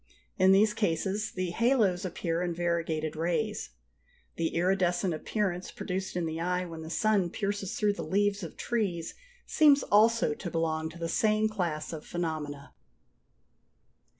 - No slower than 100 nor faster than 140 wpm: No, average, 150 wpm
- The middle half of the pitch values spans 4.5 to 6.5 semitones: No, average, 3.8 semitones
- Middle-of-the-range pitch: Yes, medium, 180 Hz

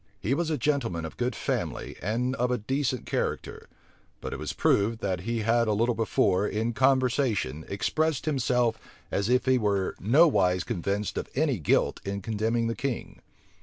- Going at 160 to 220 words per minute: Yes, average, 170 wpm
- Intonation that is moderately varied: Yes, average, 4.3 semitones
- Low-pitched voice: Yes, low, 115 Hz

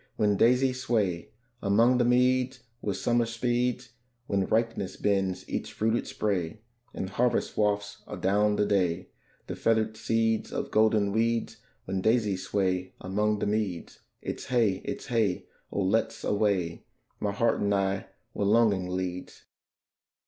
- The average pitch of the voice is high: No, low, 105 Hz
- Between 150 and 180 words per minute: No, average, 140 wpm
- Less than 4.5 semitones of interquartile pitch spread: Yes, average, 3.1 semitones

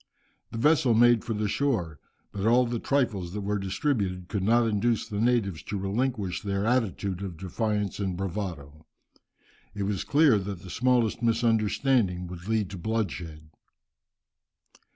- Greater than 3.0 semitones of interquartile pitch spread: Yes, average, 3.8 semitones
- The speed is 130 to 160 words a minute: Yes, average, 150 wpm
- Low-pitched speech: Yes, low, 105 Hz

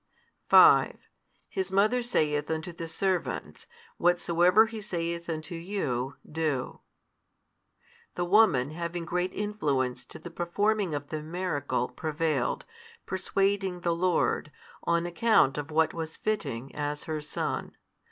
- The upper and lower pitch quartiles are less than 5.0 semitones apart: Yes, average, 3.8 semitones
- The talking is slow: Yes, slow, 125 wpm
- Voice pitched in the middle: Yes, medium, 170 Hz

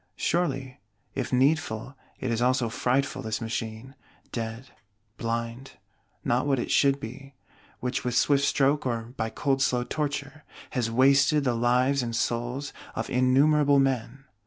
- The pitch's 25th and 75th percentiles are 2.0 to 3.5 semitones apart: Yes, average, 2.8 semitones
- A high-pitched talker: No, low, 130 Hz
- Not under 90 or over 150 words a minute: Yes, average, 140 wpm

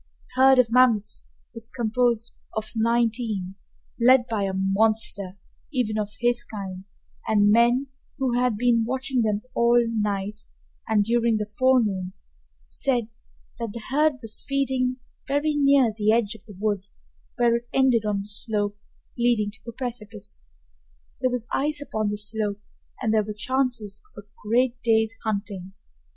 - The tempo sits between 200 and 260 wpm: No, average, 155 wpm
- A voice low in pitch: No, high, 225 Hz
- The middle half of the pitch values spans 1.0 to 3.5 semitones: Yes, average, 3.0 semitones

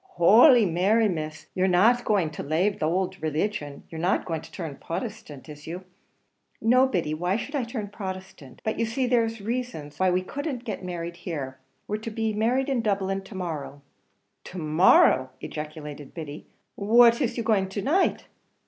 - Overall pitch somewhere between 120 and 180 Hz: No, high, 190 Hz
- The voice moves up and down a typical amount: No, wide, 6.0 semitones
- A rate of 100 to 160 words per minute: No, average, 190 wpm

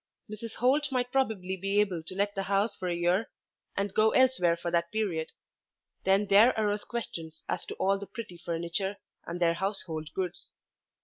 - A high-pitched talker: Yes, high, 195 Hz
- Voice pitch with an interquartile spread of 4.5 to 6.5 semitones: No, average, 3.8 semitones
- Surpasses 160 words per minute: Yes, average, 180 wpm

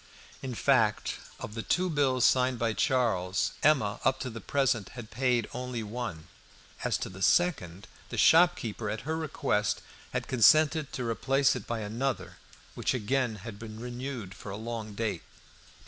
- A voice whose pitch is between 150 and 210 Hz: No, low, 120 Hz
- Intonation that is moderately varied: Yes, average, 3.8 semitones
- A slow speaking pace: No, average, 160 wpm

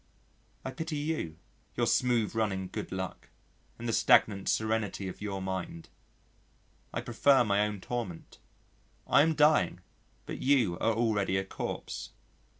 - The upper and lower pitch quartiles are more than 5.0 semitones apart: No, average, 4.6 semitones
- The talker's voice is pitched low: Yes, low, 110 Hz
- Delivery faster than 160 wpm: No, average, 140 wpm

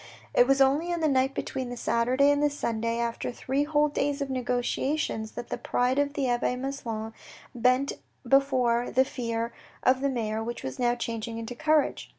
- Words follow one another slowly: No, average, 185 wpm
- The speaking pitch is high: Yes, very high, 255 Hz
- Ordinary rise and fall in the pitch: Yes, average, 3.0 semitones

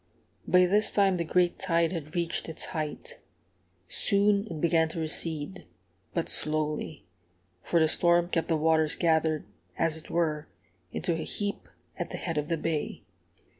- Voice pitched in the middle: Yes, medium, 165 Hz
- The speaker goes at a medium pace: Yes, average, 160 wpm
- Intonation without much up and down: Yes, narrow, 2.1 semitones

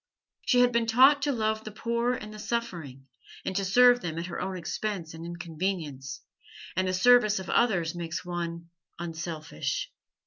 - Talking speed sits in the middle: Yes, average, 170 wpm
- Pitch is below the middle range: No, high, 190 Hz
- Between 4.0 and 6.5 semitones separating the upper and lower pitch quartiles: Yes, wide, 5.6 semitones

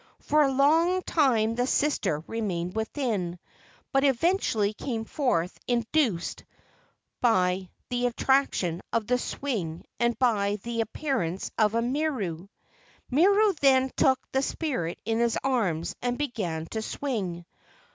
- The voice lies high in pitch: Yes, high, 235 Hz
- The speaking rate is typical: No, slow, 125 wpm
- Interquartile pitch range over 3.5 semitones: Yes, wide, 5.5 semitones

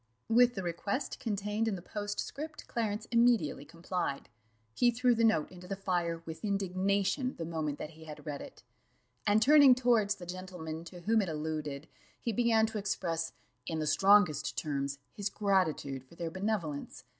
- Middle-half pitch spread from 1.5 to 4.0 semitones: No, wide, 5.4 semitones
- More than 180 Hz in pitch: Yes, high, 190 Hz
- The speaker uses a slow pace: No, average, 165 wpm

